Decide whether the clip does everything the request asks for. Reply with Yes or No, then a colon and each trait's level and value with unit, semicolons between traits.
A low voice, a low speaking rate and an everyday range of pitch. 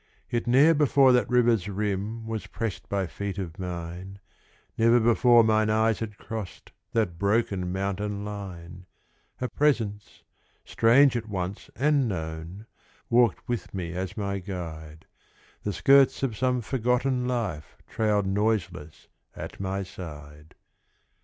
Yes: low, 105 Hz; slow, 130 wpm; average, 4.3 semitones